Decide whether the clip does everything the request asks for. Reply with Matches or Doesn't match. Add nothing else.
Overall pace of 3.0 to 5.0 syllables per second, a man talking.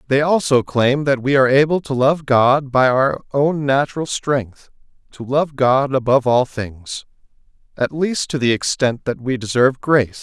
Matches